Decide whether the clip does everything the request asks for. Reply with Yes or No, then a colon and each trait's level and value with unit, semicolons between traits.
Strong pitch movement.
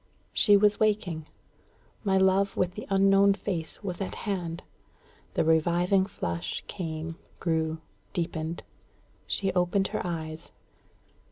No: average, 3.3 semitones